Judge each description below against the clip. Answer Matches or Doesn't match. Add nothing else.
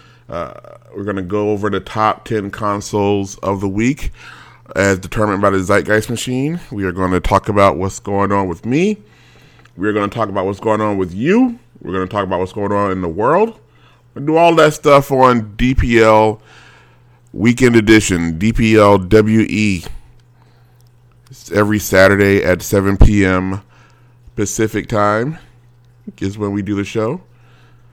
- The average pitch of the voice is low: Matches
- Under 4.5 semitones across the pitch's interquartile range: Matches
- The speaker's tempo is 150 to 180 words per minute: Matches